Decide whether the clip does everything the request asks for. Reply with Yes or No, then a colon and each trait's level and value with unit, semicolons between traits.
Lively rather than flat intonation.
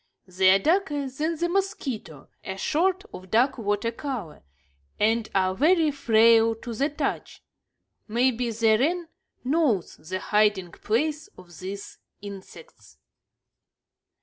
Yes: wide, 7.0 semitones